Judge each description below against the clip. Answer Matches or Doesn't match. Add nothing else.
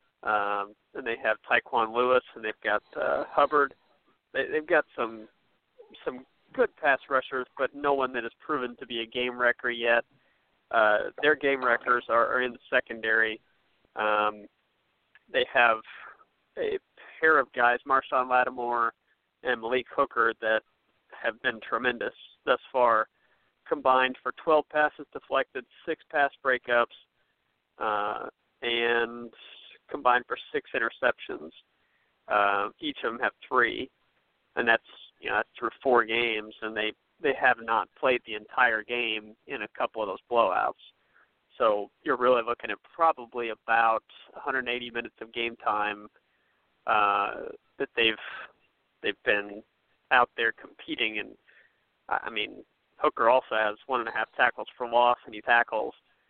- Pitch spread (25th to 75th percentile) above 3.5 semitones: Doesn't match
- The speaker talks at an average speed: Matches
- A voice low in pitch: Matches